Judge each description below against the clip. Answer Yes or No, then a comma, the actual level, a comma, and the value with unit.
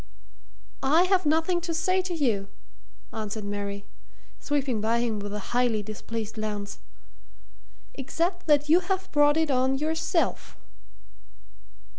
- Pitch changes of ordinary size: No, wide, 7.2 semitones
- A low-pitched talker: No, very high, 270 Hz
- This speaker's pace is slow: Yes, slow, 125 wpm